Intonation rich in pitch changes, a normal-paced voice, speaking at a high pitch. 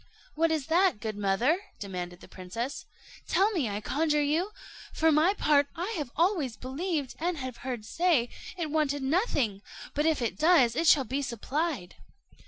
Yes: wide, 5.7 semitones; average, 165 wpm; very high, 290 Hz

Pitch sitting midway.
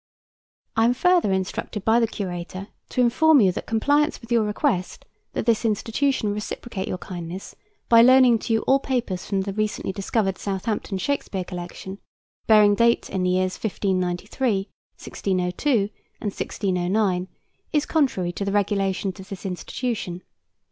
No: high, 205 Hz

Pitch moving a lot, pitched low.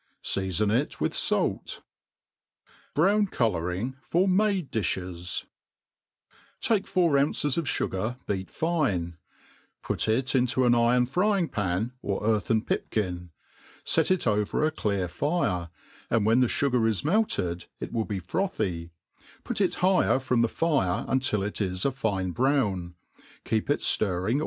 Yes: wide, 7.4 semitones; low, 115 Hz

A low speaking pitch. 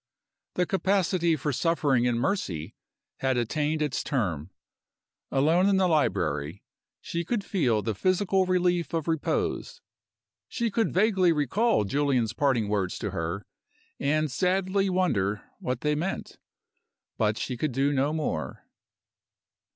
No: medium, 150 Hz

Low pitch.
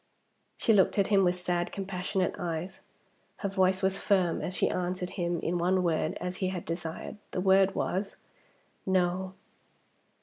No: medium, 185 Hz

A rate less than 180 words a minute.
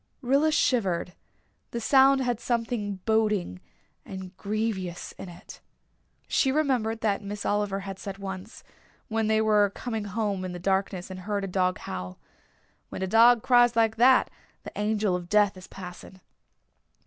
Yes: average, 150 wpm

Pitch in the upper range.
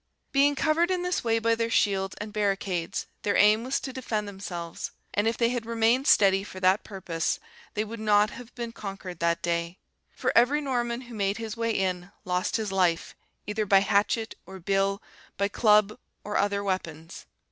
Yes: high, 210 Hz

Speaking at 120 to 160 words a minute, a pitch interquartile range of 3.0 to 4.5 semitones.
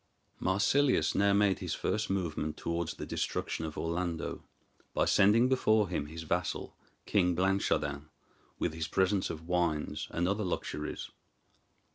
Yes: slow, 135 wpm; average, 3.6 semitones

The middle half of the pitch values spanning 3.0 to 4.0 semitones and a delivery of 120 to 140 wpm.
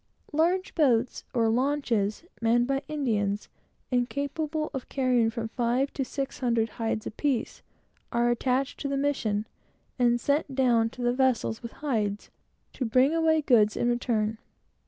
Yes: average, 3.6 semitones; slow, 135 wpm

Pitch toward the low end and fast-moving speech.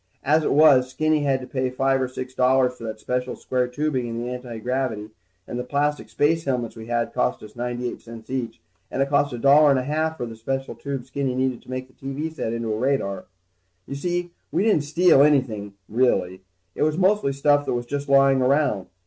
Yes: low, 130 Hz; fast, 225 wpm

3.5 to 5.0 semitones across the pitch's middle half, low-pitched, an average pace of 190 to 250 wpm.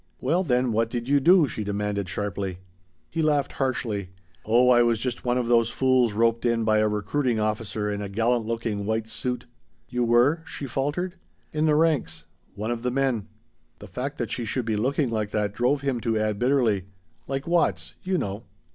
Yes: average, 4.0 semitones; low, 120 Hz; average, 200 wpm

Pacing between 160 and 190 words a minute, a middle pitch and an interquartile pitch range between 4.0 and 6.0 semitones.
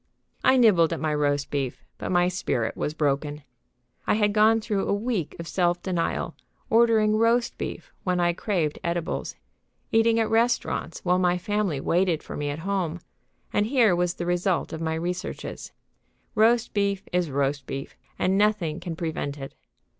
Yes: average, 170 wpm; medium, 180 Hz; average, 4.8 semitones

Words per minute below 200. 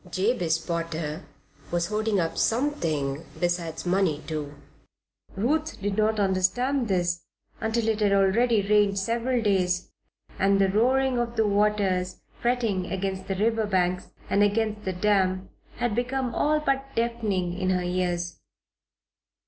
Yes: slow, 135 wpm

